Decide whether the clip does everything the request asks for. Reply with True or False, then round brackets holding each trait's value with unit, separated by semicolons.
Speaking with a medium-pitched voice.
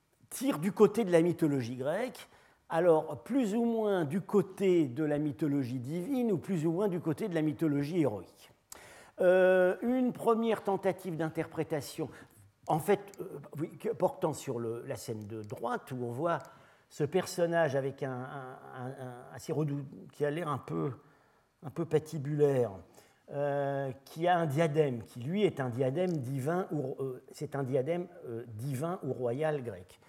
True (155 Hz)